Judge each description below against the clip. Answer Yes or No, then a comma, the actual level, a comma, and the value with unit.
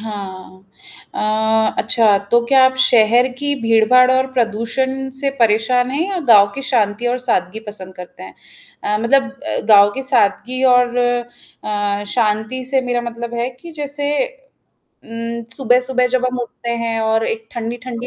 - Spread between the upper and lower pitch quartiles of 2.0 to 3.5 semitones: Yes, average, 2.8 semitones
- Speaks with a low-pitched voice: No, high, 235 Hz